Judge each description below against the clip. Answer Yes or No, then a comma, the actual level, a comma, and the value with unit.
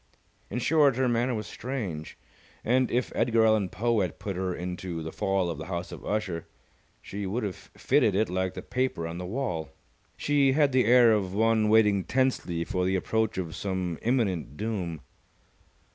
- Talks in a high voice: No, low, 105 Hz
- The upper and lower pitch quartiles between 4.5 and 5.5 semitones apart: Yes, average, 4.9 semitones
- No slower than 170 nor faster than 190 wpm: Yes, average, 180 wpm